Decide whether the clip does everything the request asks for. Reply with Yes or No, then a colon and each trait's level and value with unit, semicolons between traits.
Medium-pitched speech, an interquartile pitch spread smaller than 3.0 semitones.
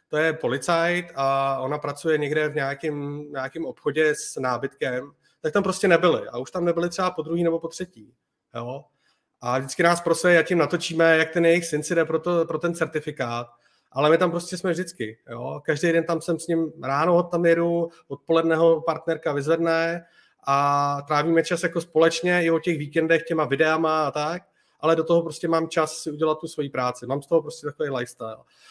Yes: medium, 160 Hz; narrow, 2.5 semitones